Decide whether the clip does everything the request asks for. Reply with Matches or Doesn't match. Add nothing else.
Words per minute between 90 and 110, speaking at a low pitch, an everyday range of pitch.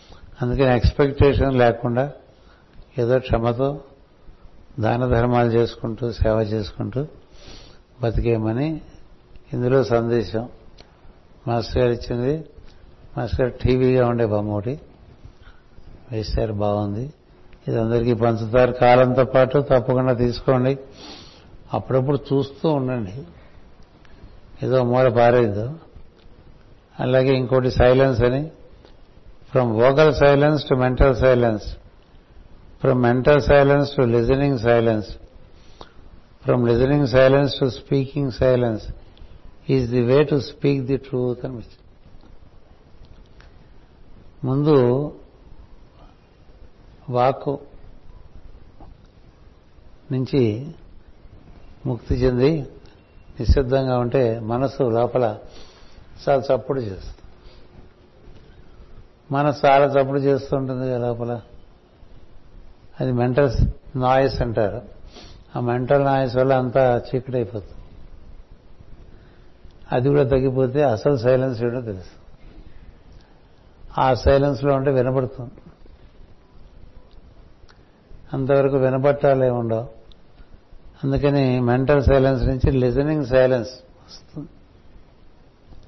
Doesn't match